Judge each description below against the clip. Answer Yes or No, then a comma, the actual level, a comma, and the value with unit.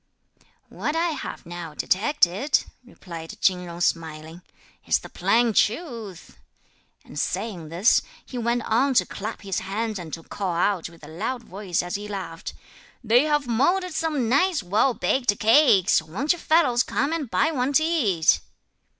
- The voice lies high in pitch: Yes, high, 220 Hz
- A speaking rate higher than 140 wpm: Yes, average, 160 wpm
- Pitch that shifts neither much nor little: No, wide, 7.5 semitones